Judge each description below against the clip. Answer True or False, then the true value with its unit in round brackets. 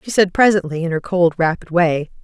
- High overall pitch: False (175 Hz)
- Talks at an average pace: False (215 wpm)